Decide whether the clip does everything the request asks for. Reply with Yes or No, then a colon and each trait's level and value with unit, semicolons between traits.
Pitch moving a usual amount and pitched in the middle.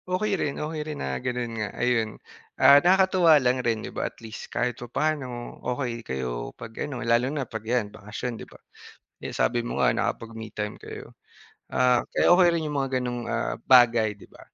No: average, 4.0 semitones; low, 125 Hz